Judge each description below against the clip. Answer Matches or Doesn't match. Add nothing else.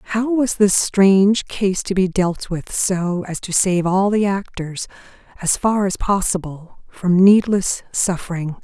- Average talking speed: Matches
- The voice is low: Doesn't match